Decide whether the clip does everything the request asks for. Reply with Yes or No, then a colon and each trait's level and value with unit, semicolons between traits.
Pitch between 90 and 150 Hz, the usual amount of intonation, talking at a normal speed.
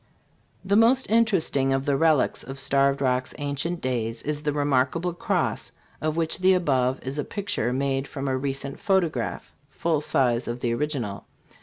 Yes: medium, 140 Hz; average, 3.9 semitones; average, 170 wpm